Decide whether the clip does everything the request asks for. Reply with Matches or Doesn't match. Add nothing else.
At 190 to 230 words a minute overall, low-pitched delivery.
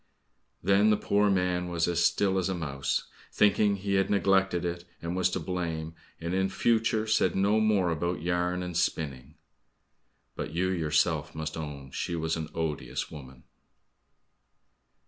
Doesn't match